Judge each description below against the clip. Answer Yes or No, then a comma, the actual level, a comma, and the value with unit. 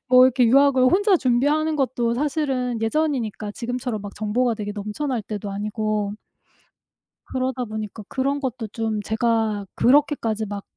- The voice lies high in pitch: Yes, high, 240 Hz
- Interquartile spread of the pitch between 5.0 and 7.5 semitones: No, average, 3.7 semitones